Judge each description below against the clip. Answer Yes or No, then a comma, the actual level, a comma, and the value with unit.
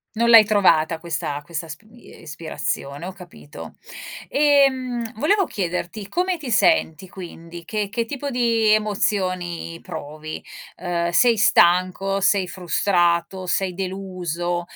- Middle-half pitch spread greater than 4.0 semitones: Yes, average, 4.5 semitones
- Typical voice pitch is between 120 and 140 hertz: No, medium, 185 Hz